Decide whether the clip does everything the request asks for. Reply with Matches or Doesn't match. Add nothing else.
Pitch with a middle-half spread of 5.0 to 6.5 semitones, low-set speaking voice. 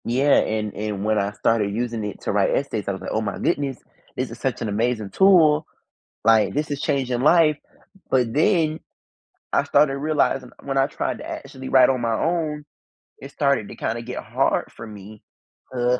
Matches